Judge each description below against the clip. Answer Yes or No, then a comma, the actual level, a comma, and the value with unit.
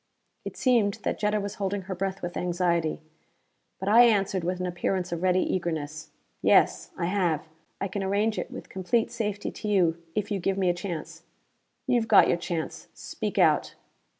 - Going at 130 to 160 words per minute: No, average, 180 wpm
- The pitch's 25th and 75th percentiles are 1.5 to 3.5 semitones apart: Yes, average, 3.0 semitones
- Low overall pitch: No, high, 190 Hz